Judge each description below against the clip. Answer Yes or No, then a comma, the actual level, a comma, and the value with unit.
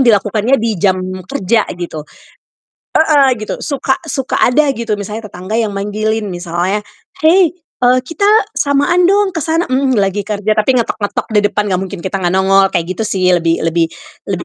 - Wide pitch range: Yes, wide, 5.9 semitones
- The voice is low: No, high, 215 Hz